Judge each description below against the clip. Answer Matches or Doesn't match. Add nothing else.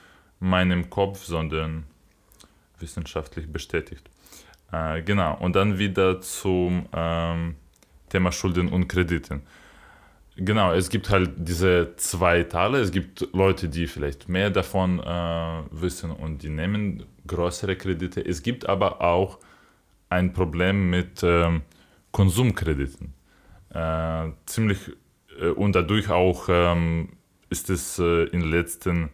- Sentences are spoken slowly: Matches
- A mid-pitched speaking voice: Doesn't match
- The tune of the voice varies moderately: Doesn't match